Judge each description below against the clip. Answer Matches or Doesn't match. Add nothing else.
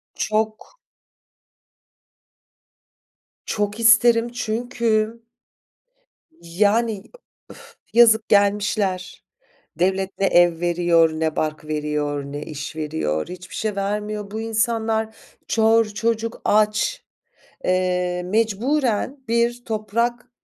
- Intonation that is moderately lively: Matches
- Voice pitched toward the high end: Matches